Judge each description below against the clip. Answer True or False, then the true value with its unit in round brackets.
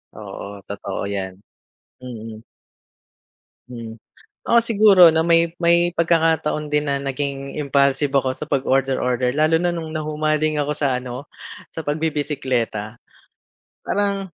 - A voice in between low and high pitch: True (145 Hz)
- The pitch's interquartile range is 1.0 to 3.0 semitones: False (3.9 semitones)